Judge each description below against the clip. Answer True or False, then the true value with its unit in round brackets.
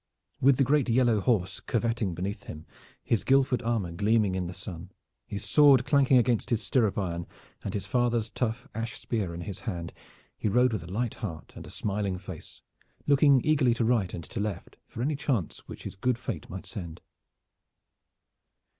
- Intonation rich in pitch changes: False (4.7 semitones)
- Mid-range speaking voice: False (110 Hz)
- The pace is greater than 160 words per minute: True (180 wpm)